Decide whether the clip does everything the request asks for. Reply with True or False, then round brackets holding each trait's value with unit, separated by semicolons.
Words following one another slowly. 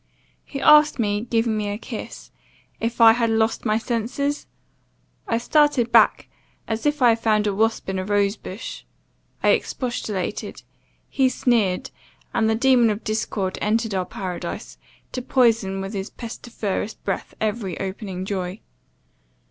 False (150 wpm)